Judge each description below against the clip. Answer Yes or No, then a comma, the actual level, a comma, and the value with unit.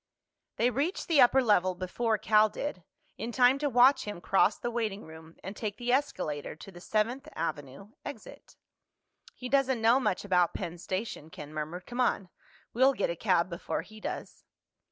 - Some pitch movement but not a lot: No, wide, 5.7 semitones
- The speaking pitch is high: Yes, high, 215 Hz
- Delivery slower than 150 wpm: No, average, 175 wpm